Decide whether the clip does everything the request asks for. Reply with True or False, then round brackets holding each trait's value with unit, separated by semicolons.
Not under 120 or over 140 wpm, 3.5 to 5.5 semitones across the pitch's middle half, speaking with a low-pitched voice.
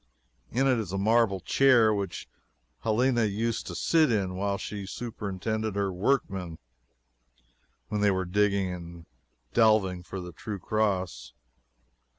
False (135 wpm; 3.0 semitones; 100 Hz)